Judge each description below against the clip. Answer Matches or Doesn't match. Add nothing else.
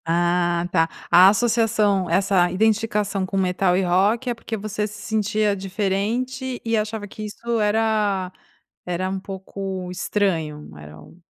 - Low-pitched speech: Doesn't match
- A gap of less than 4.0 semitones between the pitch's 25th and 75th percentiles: Matches